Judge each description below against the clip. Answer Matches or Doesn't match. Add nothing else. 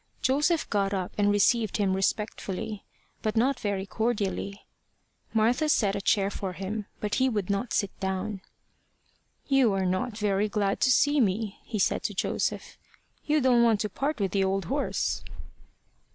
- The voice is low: Doesn't match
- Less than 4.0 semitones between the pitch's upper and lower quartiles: Matches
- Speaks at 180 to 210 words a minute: Doesn't match